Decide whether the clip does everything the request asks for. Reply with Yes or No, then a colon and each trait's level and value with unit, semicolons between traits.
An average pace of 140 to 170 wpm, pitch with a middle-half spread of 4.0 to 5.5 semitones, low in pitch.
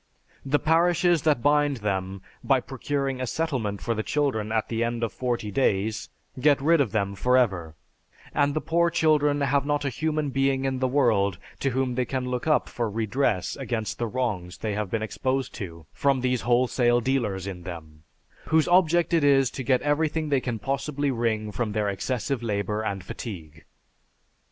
No: average, 185 wpm; average, 4.9 semitones; low, 125 Hz